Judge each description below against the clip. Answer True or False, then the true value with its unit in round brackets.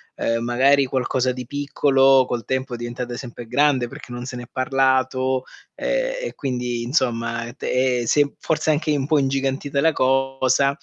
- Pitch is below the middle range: True (130 Hz)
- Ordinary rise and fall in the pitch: False (2.1 semitones)